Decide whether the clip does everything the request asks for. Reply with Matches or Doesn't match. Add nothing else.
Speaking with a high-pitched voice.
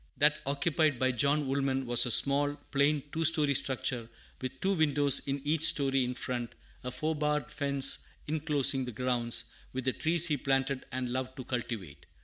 Doesn't match